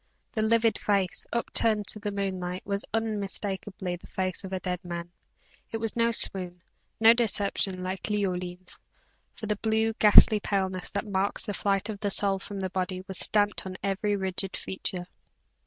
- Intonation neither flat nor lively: No, narrow, 2.2 semitones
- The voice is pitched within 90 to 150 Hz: No, high, 195 Hz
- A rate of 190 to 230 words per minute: No, average, 170 wpm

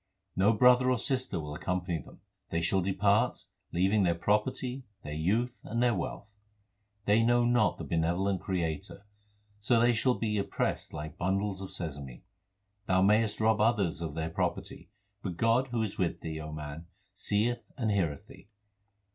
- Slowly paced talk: No, average, 165 wpm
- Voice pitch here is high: No, low, 100 Hz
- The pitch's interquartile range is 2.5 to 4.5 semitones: No, average, 5.2 semitones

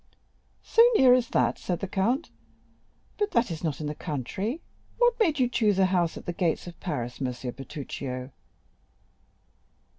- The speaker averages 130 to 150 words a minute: No, average, 160 wpm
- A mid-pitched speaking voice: Yes, medium, 180 Hz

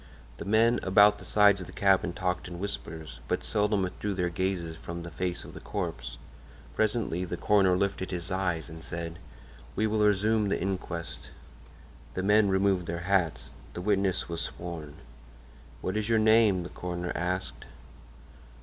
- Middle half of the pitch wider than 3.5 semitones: No, average, 2.9 semitones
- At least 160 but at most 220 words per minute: Yes, average, 165 wpm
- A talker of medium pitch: No, very low, 95 Hz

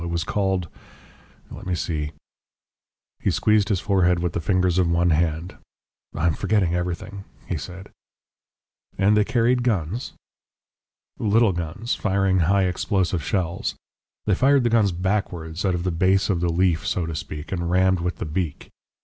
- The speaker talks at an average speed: Yes, average, 165 wpm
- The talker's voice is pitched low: Yes, very low, 90 Hz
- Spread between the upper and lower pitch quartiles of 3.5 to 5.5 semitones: No, average, 2.7 semitones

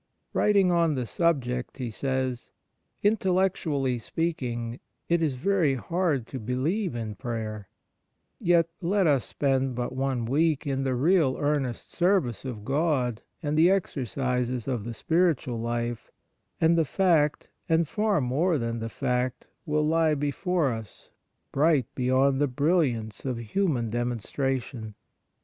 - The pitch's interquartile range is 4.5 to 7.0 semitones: Yes, average, 5.2 semitones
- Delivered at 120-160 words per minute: Yes, average, 140 wpm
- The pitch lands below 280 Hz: Yes, low, 135 Hz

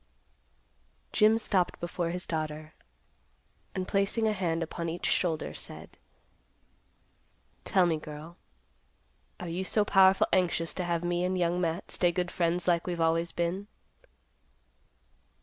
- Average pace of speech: No, slow, 130 wpm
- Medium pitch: Yes, medium, 175 Hz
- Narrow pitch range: Yes, narrow, 1.9 semitones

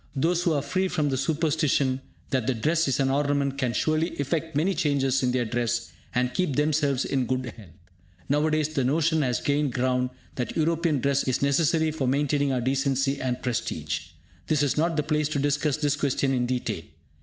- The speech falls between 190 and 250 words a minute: Yes, average, 195 wpm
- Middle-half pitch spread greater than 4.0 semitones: No, average, 3.1 semitones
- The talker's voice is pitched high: No, medium, 140 Hz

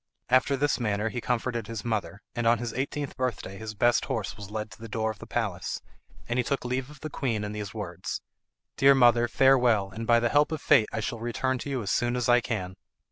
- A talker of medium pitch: No, low, 120 Hz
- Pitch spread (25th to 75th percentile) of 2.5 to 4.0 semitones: Yes, average, 2.9 semitones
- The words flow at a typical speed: No, fast, 240 wpm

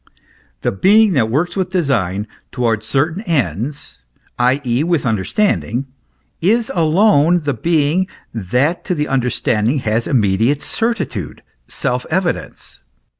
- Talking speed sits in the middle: No, slow, 115 wpm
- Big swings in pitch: Yes, wide, 7.0 semitones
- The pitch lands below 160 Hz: Yes, medium, 140 Hz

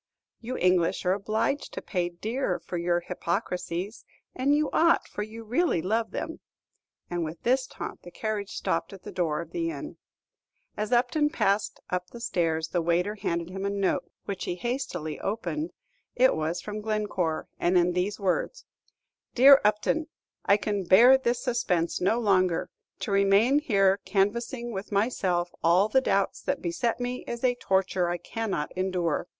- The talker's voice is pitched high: Yes, high, 200 Hz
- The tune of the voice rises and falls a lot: No, average, 5.0 semitones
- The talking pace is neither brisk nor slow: Yes, average, 165 wpm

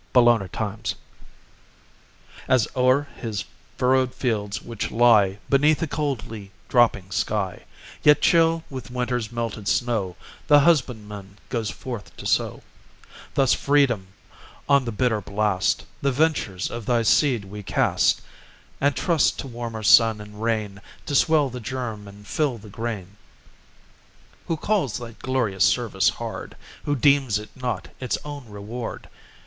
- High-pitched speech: No, low, 120 Hz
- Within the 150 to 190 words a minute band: No, average, 140 wpm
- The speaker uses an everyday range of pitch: Yes, average, 4.2 semitones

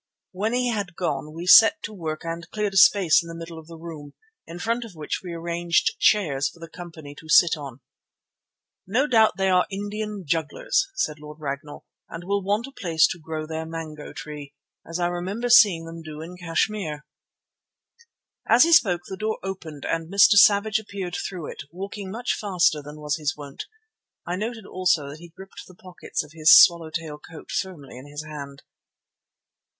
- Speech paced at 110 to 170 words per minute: No, average, 190 wpm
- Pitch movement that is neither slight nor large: Yes, average, 4.4 semitones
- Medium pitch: Yes, medium, 170 Hz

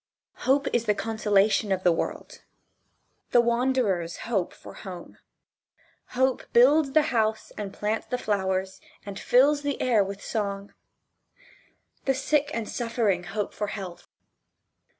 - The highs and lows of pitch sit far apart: No, average, 4.2 semitones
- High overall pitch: Yes, high, 220 Hz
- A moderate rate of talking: No, slow, 130 wpm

